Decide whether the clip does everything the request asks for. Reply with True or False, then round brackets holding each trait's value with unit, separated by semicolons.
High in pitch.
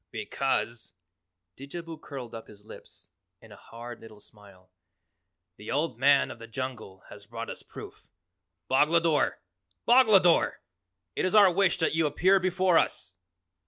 False (135 Hz)